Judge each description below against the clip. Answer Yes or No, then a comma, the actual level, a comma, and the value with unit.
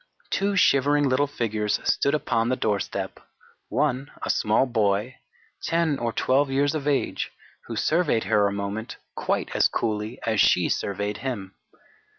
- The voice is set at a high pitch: No, low, 125 Hz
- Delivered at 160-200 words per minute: No, average, 150 wpm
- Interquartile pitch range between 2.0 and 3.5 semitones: No, average, 5.2 semitones